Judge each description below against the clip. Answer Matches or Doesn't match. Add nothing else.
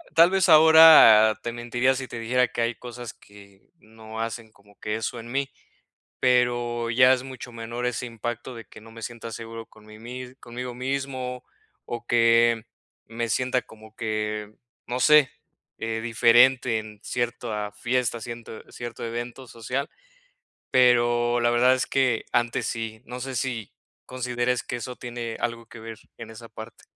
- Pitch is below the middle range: Matches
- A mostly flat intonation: Matches